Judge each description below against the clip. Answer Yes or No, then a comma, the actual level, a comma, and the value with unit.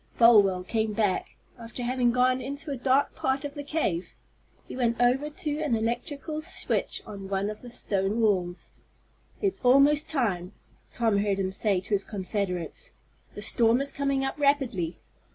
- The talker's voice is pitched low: No, high, 235 Hz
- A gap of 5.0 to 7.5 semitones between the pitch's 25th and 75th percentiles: Yes, wide, 5.6 semitones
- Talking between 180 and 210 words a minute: No, average, 165 wpm